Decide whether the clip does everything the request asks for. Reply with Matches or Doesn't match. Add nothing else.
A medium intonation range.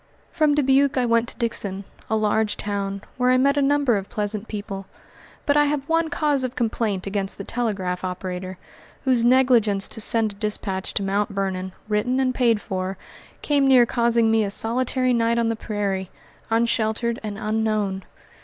Matches